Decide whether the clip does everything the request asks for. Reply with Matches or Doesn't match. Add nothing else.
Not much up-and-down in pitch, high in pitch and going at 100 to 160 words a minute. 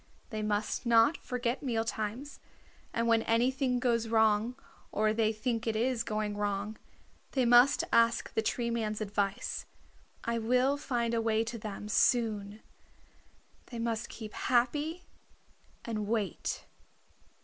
Matches